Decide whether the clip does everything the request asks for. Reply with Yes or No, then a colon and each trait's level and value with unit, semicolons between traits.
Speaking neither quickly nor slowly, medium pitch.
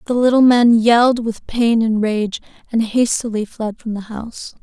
No: average, 180 wpm; high, 225 Hz